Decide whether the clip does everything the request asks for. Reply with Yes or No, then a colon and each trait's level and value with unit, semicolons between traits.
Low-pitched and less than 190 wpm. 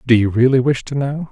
No: low, 130 Hz; fast, 275 wpm